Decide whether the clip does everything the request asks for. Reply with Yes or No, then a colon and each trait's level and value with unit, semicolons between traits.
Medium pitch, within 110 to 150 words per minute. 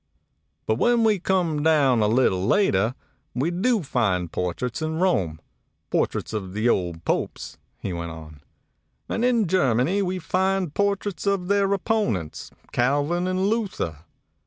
Yes: medium, 155 Hz; average, 140 wpm